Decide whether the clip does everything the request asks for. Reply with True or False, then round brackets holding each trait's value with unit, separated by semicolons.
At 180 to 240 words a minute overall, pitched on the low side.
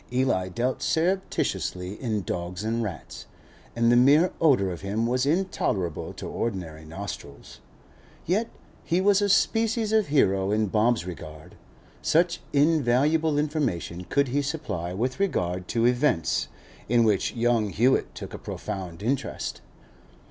False (135 wpm; 120 Hz)